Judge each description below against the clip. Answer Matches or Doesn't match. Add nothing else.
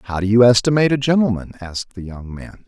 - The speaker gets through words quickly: Matches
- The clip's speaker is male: Matches